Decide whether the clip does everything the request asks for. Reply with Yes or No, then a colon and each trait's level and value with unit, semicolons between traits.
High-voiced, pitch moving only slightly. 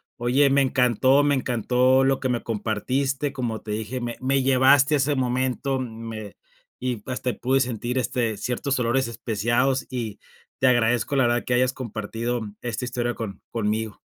No: low, 125 Hz; narrow, 2.3 semitones